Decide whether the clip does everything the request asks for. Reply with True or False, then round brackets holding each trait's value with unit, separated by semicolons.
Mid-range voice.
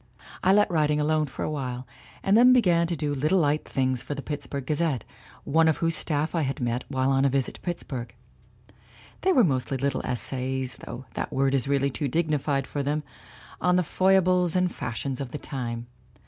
True (145 Hz)